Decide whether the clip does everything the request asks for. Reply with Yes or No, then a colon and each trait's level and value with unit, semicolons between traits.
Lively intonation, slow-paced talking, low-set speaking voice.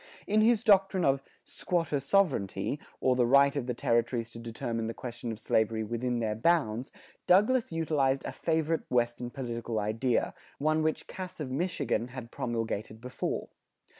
No: wide, 5.7 semitones; average, 155 wpm; low, 130 Hz